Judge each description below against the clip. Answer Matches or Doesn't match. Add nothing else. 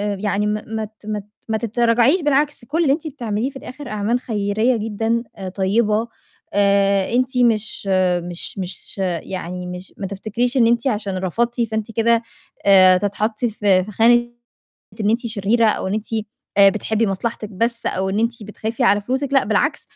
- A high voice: Matches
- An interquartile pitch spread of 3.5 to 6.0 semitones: Doesn't match